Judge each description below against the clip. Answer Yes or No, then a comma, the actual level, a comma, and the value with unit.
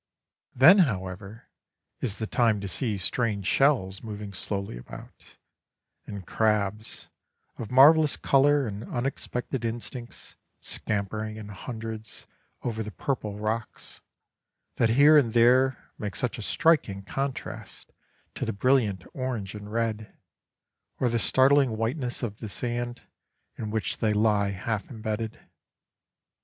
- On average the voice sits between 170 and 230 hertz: No, low, 110 Hz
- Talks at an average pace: No, slow, 125 wpm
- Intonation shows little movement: No, average, 3.4 semitones